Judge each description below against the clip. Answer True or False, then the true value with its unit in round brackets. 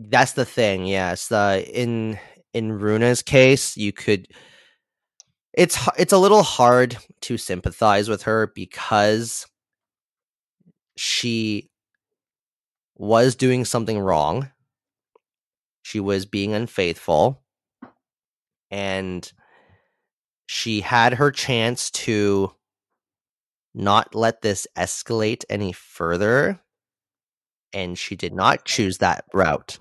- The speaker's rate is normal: False (100 wpm)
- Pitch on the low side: True (110 Hz)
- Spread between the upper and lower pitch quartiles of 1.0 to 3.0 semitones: False (3.6 semitones)